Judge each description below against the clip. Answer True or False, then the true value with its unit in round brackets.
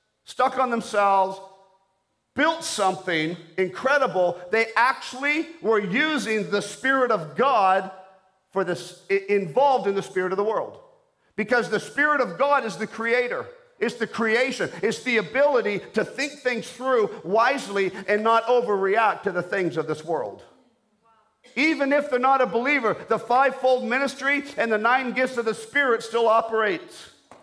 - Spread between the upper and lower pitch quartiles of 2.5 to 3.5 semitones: False (5.0 semitones)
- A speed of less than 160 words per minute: True (150 wpm)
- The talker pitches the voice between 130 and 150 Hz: False (230 Hz)